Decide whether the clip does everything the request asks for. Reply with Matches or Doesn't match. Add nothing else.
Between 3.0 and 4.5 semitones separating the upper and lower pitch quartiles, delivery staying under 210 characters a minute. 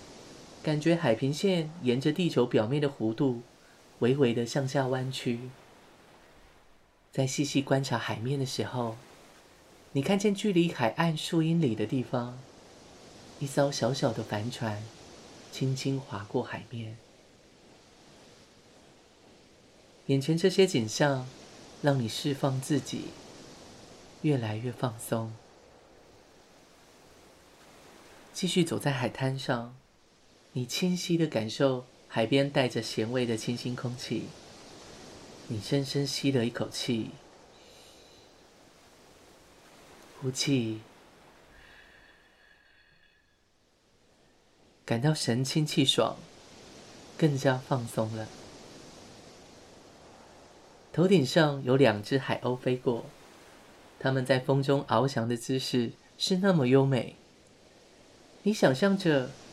Matches